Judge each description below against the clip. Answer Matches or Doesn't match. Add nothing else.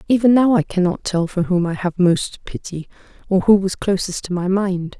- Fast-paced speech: Matches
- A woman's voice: Matches